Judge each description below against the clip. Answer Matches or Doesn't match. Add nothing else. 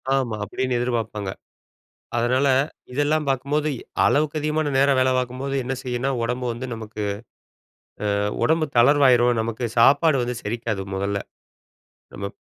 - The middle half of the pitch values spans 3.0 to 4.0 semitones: Matches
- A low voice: Matches